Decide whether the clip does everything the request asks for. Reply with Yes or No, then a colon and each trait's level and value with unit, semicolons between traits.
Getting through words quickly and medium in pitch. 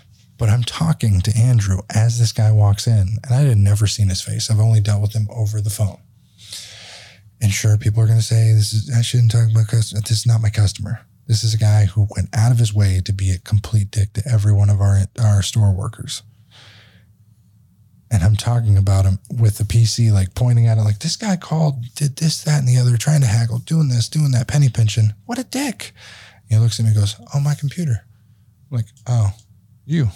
No: fast, 225 wpm; low, 110 Hz